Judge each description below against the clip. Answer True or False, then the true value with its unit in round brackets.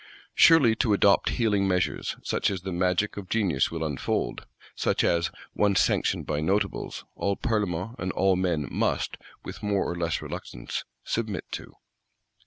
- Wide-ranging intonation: False (3.1 semitones)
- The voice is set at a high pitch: False (95 Hz)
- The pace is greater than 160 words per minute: False (155 wpm)